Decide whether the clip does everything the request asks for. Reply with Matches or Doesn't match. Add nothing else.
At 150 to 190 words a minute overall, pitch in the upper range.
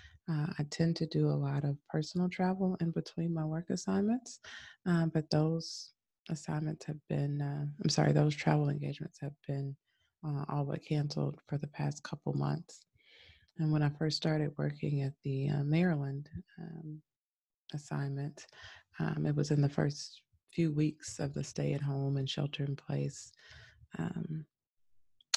Doesn't match